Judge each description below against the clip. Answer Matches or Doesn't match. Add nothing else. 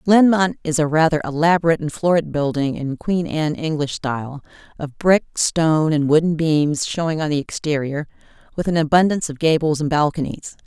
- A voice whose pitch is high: Doesn't match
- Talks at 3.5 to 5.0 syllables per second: Doesn't match